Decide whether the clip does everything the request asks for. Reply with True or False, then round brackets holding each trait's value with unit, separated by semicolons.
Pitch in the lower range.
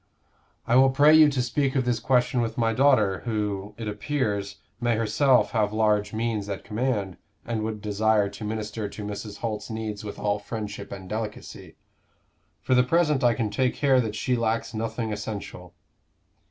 True (110 Hz)